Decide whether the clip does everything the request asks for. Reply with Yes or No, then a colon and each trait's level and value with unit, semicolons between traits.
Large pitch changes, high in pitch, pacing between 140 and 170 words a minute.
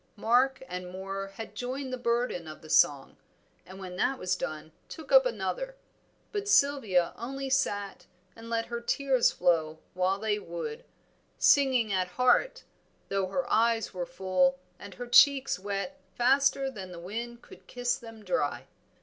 Yes: wide, 6.1 semitones; high, 225 Hz; average, 160 wpm